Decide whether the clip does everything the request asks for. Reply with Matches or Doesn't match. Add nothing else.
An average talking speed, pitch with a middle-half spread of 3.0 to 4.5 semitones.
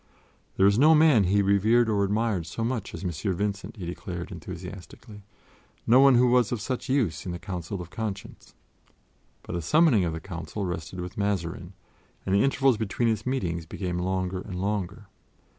Matches